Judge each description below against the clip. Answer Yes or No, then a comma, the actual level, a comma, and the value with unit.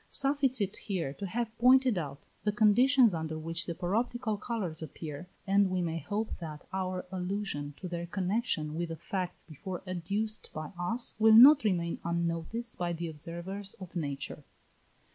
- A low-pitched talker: No, medium, 185 Hz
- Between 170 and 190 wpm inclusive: No, average, 160 wpm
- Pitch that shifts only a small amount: No, average, 4.6 semitones